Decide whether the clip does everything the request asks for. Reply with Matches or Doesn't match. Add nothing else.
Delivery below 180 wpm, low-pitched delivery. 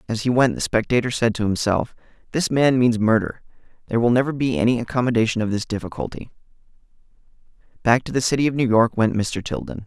Doesn't match